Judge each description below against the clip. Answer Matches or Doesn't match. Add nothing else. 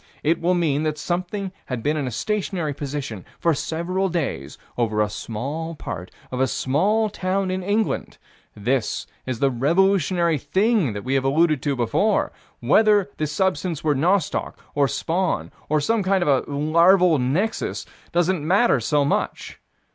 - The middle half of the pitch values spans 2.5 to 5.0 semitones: Doesn't match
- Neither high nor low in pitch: Matches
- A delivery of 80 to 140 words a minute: Doesn't match